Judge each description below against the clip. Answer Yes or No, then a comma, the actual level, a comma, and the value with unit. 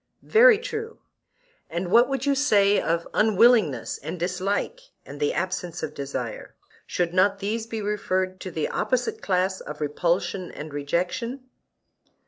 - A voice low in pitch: No, high, 190 Hz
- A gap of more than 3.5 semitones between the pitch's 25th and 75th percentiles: Yes, wide, 5.4 semitones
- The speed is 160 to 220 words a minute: No, average, 140 wpm